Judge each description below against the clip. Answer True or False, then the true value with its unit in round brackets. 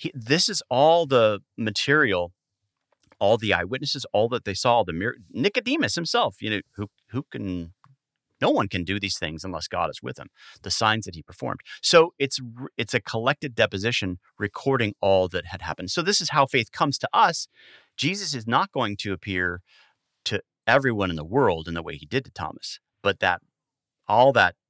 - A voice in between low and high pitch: False (115 Hz)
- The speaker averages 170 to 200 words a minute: True (190 wpm)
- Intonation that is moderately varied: False (6.4 semitones)